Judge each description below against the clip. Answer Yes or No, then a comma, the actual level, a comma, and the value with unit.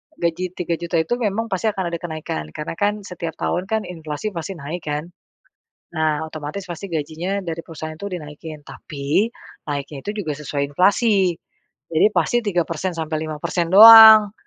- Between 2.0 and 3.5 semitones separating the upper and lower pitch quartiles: No, average, 4.0 semitones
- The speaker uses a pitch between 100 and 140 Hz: No, medium, 170 Hz